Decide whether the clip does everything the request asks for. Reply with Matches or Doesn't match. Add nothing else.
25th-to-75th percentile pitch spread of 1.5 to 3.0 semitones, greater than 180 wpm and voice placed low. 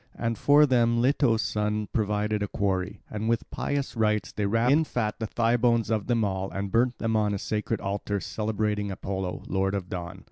Matches